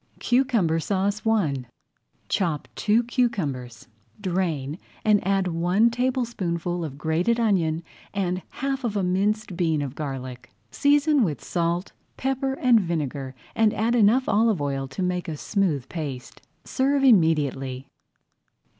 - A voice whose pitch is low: No, medium, 185 Hz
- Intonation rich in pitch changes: Yes, wide, 6.7 semitones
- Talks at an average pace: No, slow, 130 wpm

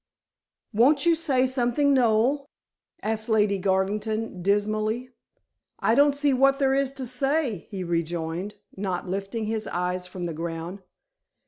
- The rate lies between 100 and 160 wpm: Yes, slow, 135 wpm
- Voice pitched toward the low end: No, high, 220 Hz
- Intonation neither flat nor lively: No, wide, 5.8 semitones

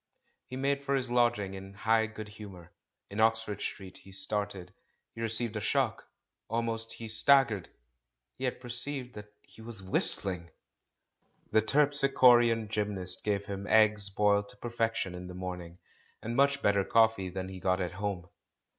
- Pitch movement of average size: Yes, average, 3.4 semitones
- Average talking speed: Yes, average, 160 wpm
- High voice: No, low, 105 Hz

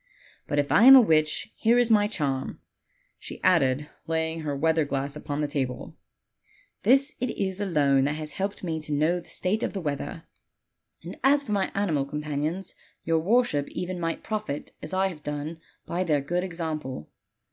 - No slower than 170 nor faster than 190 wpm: Yes, average, 185 wpm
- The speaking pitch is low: No, medium, 160 Hz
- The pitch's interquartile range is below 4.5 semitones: No, average, 4.8 semitones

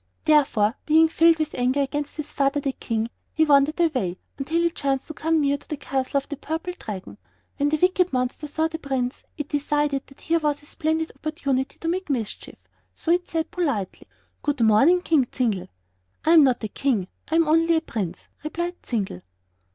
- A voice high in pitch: Yes, very high, 290 Hz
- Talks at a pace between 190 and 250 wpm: Yes, average, 195 wpm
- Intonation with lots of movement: No, average, 3.6 semitones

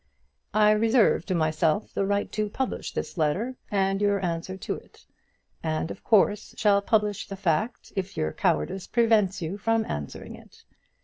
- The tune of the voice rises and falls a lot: No, average, 3.7 semitones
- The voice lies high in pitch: Yes, high, 200 Hz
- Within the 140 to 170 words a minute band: Yes, average, 165 wpm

